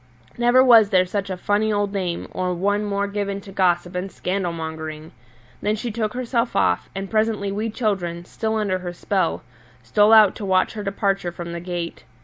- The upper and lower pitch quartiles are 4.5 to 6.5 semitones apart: No, average, 2.9 semitones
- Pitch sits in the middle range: No, high, 200 Hz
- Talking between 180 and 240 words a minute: Yes, average, 190 wpm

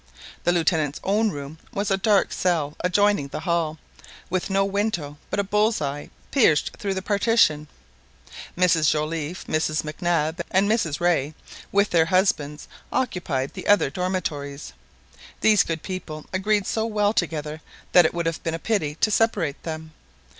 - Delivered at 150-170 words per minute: Yes, average, 160 wpm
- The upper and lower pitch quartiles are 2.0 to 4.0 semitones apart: No, average, 4.6 semitones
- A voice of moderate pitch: Yes, medium, 175 Hz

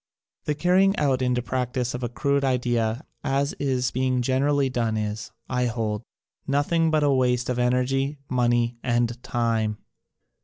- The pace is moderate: Yes, average, 150 wpm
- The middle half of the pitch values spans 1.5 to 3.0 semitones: Yes, narrow, 2.6 semitones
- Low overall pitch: Yes, low, 125 Hz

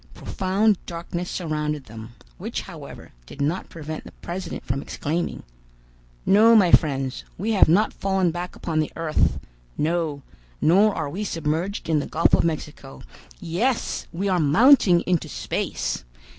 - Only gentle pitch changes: No, average, 4.0 semitones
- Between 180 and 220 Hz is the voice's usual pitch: No, medium, 170 Hz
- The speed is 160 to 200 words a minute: No, average, 145 wpm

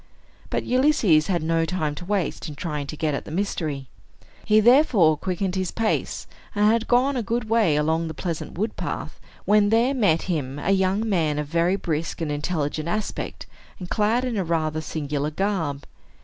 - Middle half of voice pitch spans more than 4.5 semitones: Yes, wide, 5.4 semitones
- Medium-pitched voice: Yes, medium, 175 Hz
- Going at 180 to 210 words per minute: Yes, average, 185 wpm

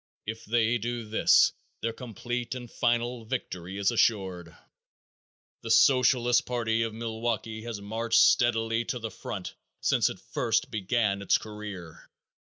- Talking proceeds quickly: No, slow, 135 wpm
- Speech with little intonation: Yes, narrow, 2.0 semitones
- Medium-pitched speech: No, low, 115 Hz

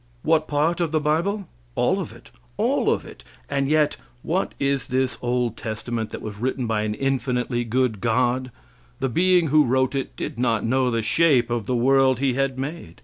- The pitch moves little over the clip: No, average, 3.6 semitones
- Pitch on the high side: No, low, 130 Hz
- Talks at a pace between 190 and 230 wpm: Yes, average, 195 wpm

